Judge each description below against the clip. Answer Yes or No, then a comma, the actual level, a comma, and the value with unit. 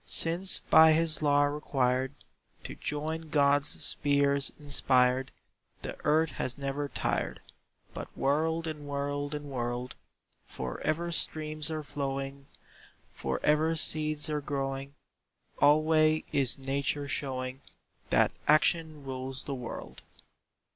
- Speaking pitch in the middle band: Yes, medium, 145 Hz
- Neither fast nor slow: No, slow, 115 wpm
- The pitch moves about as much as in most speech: No, narrow, 2.2 semitones